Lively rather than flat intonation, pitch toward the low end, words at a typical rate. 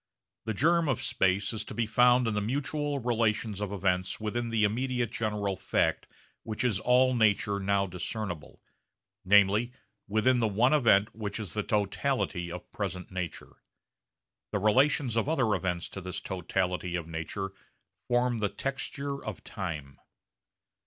No: average, 4.1 semitones; low, 105 Hz; average, 150 wpm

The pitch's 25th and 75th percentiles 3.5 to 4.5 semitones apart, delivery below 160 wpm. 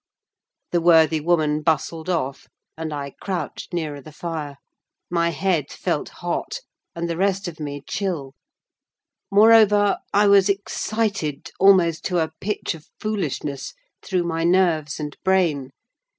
Yes: average, 3.9 semitones; slow, 135 wpm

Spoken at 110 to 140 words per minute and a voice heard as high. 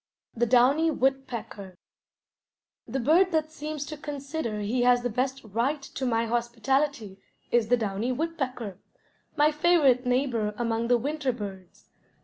Yes: slow, 135 wpm; very high, 250 Hz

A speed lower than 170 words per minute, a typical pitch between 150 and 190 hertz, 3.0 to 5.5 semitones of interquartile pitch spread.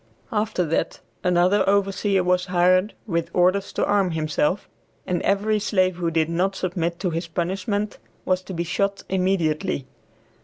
No: average, 150 wpm; medium, 185 Hz; narrow, 2.5 semitones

